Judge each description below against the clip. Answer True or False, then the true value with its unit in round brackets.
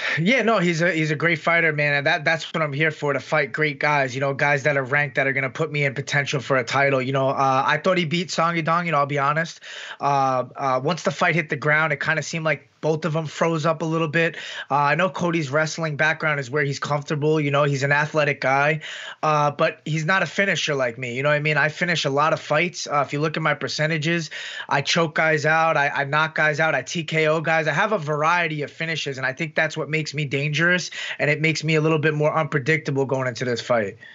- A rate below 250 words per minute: False (265 wpm)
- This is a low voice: False (155 Hz)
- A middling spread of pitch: False (2.3 semitones)